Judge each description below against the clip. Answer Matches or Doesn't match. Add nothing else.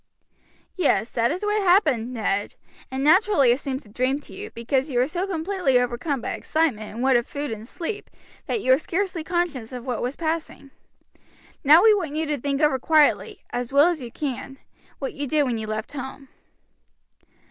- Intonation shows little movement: Doesn't match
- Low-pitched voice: Doesn't match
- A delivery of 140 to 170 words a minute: Doesn't match